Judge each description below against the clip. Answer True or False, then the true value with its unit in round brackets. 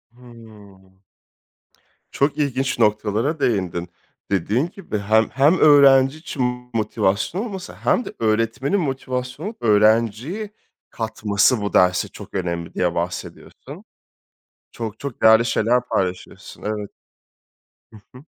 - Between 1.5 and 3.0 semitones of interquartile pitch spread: False (4.7 semitones)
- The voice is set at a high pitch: False (115 Hz)